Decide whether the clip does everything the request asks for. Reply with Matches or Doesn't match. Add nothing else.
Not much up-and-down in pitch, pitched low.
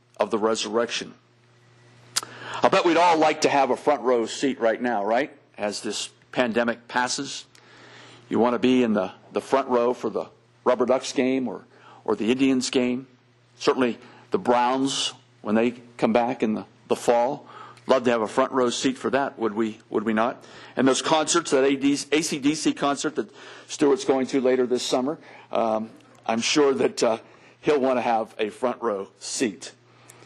Matches